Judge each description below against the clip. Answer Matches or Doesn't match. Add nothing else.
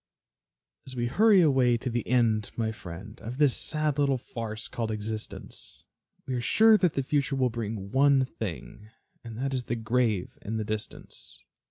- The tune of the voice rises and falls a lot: Doesn't match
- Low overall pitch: Matches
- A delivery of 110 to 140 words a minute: Doesn't match